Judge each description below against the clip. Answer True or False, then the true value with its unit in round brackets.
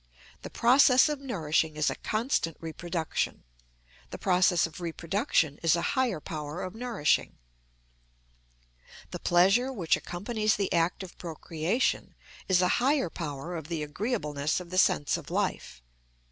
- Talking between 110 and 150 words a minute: True (140 wpm)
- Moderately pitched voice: True (175 Hz)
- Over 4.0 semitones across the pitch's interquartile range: True (5.3 semitones)